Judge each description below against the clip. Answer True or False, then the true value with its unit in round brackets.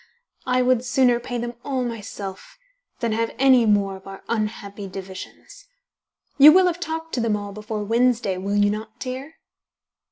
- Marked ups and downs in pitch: False (3.7 semitones)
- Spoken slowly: False (165 wpm)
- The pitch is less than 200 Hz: False (230 Hz)